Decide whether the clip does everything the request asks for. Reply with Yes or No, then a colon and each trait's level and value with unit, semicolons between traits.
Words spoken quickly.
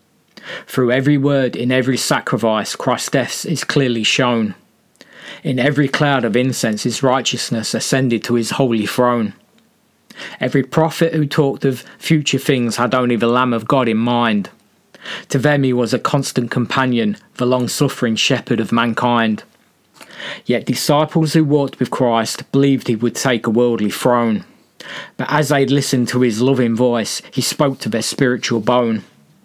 No: average, 160 wpm